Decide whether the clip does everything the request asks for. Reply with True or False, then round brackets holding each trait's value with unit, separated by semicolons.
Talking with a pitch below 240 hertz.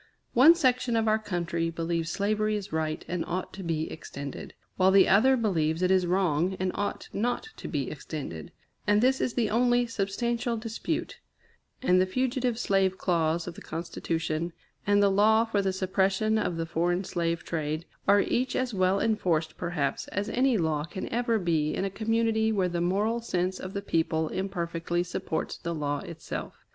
True (190 Hz)